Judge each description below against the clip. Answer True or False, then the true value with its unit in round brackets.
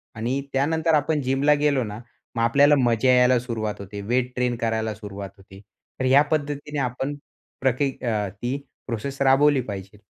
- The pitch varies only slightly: False (4.1 semitones)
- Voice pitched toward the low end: True (125 Hz)